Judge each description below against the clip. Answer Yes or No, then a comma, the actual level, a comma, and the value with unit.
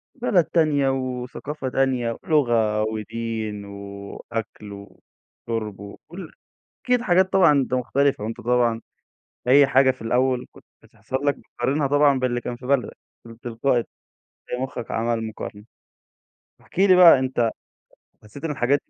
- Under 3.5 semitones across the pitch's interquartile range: No, average, 3.9 semitones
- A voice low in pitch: Yes, low, 125 Hz